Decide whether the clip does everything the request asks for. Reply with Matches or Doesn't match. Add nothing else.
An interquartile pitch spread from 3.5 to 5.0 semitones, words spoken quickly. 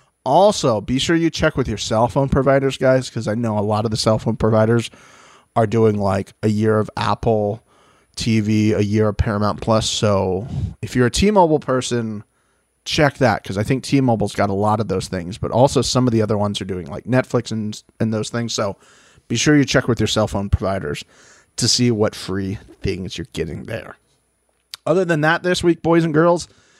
Matches